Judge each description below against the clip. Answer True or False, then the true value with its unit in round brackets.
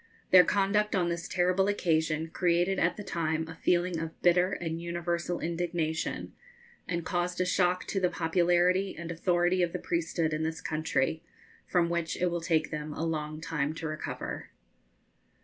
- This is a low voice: False (170 Hz)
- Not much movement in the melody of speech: True (1.7 semitones)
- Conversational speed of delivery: True (165 wpm)